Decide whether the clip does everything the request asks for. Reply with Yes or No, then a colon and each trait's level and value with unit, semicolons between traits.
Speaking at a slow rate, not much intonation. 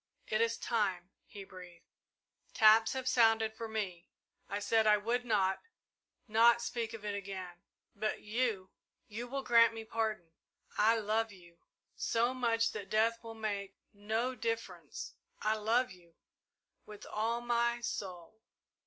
No: average, 145 wpm; narrow, 2.3 semitones